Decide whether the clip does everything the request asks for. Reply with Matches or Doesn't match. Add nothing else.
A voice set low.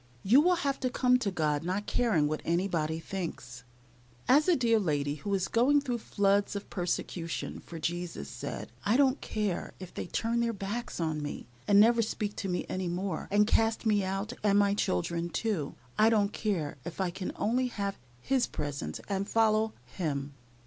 Doesn't match